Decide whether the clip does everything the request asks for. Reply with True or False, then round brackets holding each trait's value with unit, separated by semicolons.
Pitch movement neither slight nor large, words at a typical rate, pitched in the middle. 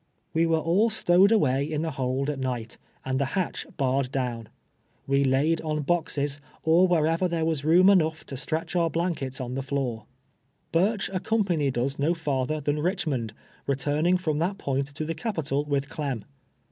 True (3.8 semitones; 175 wpm; 150 Hz)